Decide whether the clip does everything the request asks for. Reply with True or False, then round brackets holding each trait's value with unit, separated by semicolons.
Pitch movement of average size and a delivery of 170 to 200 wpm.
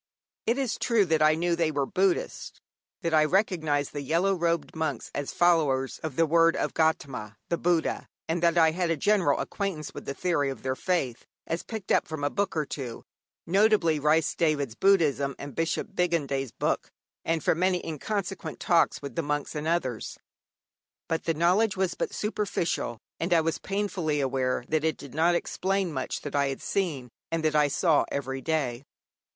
True (3.6 semitones; 185 wpm)